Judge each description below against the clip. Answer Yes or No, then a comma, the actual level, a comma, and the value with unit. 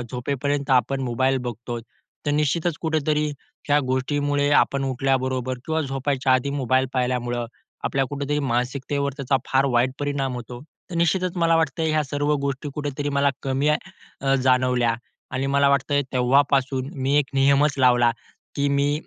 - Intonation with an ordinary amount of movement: No, narrow, 1.9 semitones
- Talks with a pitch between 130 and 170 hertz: Yes, medium, 140 Hz